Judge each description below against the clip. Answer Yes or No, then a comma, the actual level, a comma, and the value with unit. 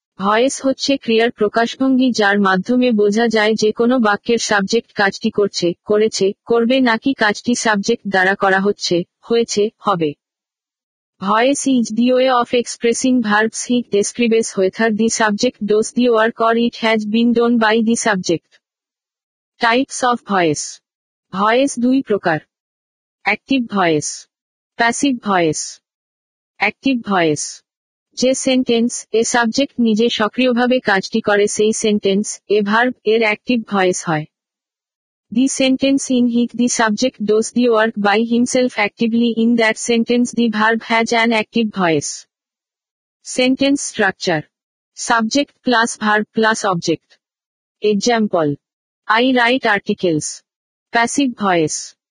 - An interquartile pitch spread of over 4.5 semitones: No, average, 3.0 semitones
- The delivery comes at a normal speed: No, fast, 125 wpm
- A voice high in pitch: Yes, high, 225 Hz